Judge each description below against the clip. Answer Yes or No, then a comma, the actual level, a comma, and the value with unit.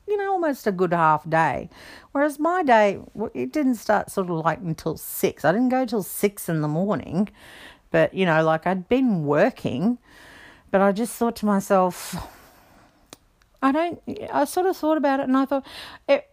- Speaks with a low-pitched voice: No, high, 215 Hz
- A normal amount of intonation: No, wide, 7.5 semitones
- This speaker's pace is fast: No, average, 185 wpm